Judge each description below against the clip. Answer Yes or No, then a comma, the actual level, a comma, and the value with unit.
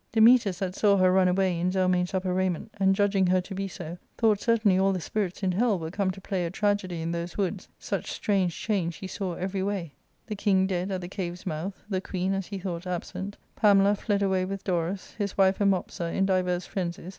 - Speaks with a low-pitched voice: No, high, 190 Hz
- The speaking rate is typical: No, fast, 225 wpm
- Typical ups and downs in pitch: No, narrow, 1.7 semitones